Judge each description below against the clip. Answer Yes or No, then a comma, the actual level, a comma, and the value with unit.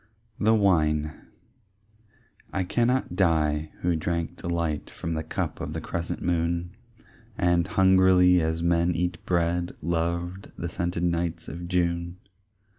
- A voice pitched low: Yes, very low, 85 Hz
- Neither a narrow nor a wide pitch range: No, narrow, 1.2 semitones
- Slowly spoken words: Yes, slow, 125 wpm